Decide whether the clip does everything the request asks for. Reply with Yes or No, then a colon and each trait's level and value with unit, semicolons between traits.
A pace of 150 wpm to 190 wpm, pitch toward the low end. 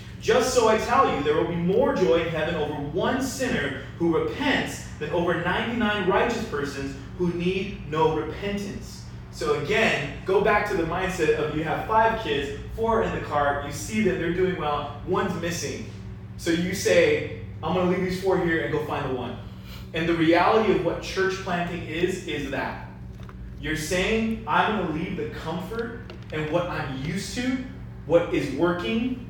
No: average, 185 wpm; medium, 170 Hz